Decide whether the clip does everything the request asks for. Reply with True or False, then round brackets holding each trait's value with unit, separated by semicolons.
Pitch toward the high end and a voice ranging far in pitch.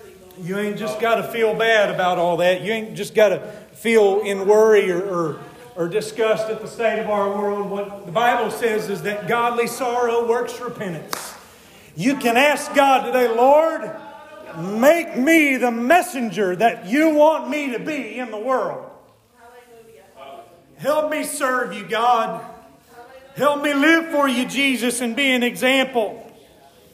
False (235 Hz; 3.8 semitones)